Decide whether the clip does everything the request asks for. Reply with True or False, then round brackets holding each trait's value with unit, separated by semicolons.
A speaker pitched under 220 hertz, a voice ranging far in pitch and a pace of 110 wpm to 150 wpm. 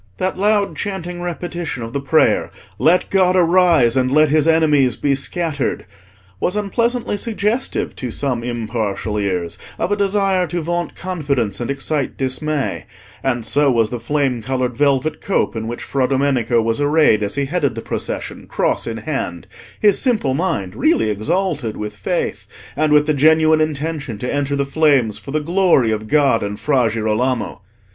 False (140 Hz; 6.2 semitones; 165 wpm)